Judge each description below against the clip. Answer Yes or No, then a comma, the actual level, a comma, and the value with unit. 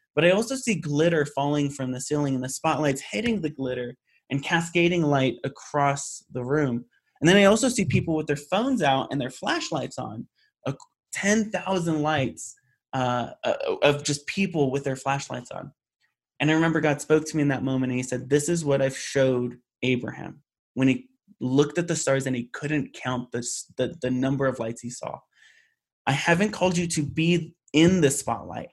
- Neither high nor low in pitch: Yes, medium, 145 Hz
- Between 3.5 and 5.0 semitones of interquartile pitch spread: Yes, average, 4.4 semitones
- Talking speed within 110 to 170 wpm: No, average, 190 wpm